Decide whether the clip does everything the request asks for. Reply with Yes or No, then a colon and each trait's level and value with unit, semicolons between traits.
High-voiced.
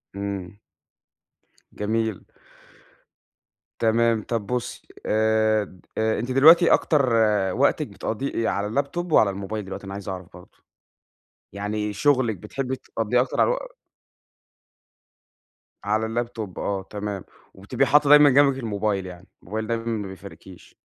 No: low, 110 Hz